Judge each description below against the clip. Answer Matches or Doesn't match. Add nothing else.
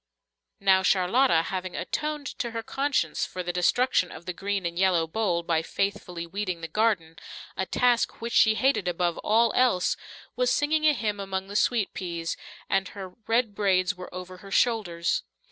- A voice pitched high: Matches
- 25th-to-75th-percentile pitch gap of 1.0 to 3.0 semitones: Doesn't match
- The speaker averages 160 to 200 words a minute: Matches